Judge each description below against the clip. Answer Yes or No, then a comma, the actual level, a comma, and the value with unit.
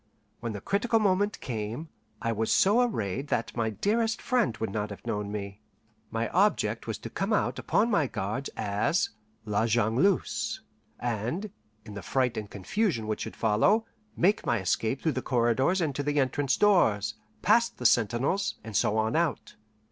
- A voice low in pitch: Yes, low, 120 Hz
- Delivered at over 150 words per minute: Yes, average, 170 wpm